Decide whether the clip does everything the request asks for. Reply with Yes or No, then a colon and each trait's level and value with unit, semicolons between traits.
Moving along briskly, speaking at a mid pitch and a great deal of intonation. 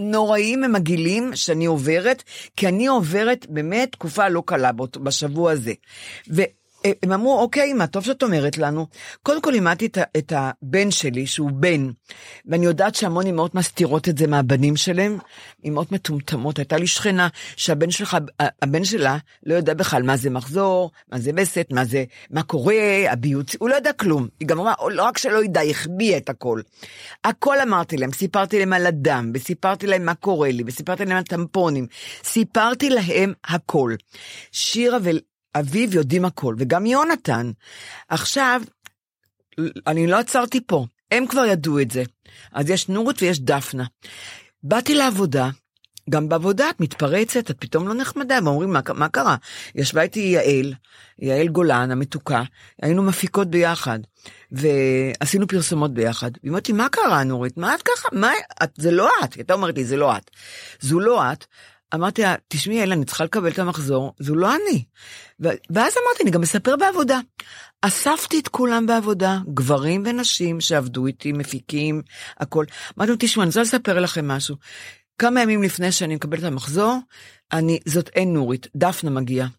Yes: fast, 165 wpm; medium, 170 Hz; wide, 6.0 semitones